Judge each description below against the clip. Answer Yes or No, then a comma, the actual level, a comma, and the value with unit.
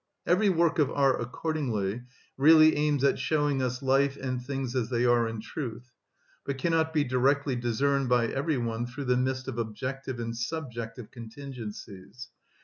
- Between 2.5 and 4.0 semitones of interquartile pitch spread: Yes, average, 3.0 semitones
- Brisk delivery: No, average, 160 wpm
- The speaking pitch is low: Yes, low, 130 Hz